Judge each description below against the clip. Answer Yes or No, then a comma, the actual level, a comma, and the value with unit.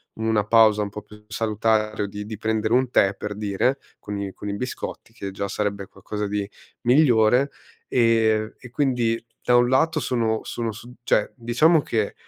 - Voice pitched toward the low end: Yes, low, 110 Hz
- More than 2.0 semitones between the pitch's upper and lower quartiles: Yes, average, 2.7 semitones